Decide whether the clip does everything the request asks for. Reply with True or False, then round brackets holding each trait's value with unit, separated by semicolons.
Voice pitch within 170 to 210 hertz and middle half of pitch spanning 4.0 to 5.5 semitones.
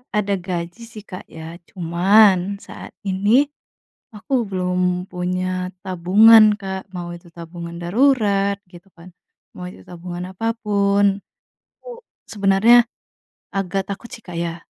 False (190 Hz; 2.6 semitones)